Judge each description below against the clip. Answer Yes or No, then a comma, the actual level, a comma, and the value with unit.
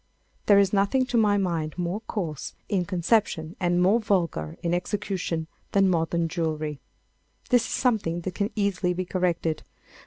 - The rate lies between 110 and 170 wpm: Yes, average, 155 wpm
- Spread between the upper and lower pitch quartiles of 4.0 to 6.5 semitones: No, average, 3.3 semitones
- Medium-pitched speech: Yes, medium, 180 Hz